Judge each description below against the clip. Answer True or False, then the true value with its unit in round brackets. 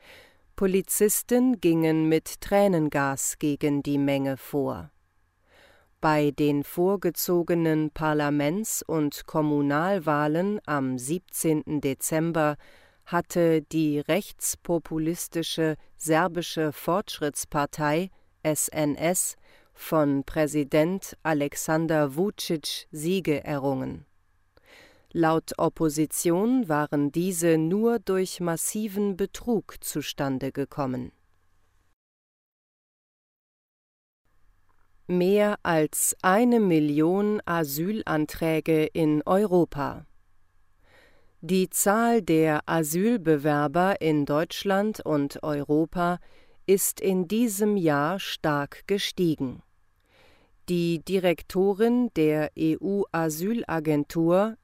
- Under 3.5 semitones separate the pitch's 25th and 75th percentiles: False (4.0 semitones)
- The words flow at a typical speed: False (70 wpm)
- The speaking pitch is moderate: True (160 Hz)